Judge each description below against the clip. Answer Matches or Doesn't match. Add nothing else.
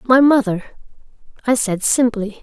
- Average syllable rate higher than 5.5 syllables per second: Doesn't match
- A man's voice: Doesn't match